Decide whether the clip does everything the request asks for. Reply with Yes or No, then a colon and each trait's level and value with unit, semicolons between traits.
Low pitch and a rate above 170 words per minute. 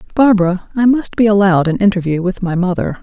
No: high, 195 Hz; average, 200 wpm